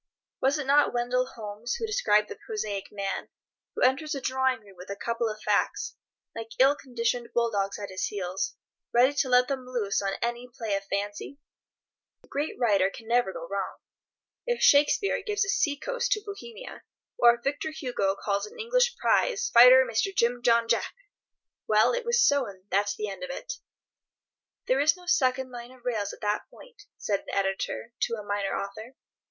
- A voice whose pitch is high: Yes, high, 240 Hz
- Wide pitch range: Yes, wide, 5.7 semitones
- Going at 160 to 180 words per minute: No, average, 190 wpm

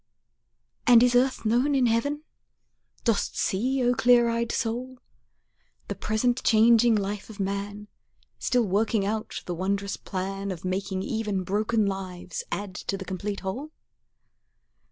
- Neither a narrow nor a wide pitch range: Yes, average, 3.6 semitones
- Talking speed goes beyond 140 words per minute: No, slow, 135 wpm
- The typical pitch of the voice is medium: No, high, 215 Hz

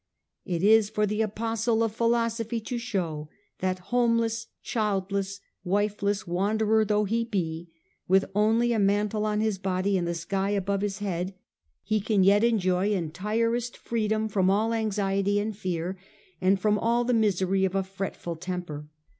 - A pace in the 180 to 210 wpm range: No, average, 155 wpm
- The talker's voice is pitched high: Yes, high, 205 Hz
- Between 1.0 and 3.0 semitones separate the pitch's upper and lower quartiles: Yes, narrow, 2.6 semitones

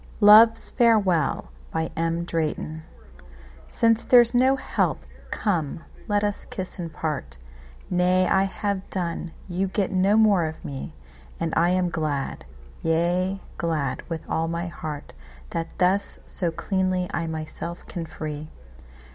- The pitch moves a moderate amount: Yes, average, 3.8 semitones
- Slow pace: Yes, slow, 115 wpm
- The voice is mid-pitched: Yes, medium, 175 Hz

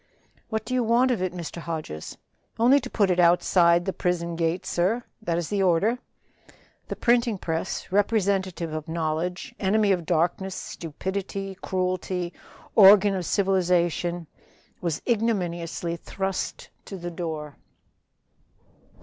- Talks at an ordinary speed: No, slow, 130 wpm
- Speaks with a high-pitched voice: No, medium, 180 Hz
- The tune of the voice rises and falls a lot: No, average, 2.9 semitones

